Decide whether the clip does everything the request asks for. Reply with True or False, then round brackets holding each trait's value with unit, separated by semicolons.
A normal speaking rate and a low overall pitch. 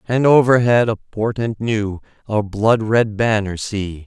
True (145 wpm; 110 Hz)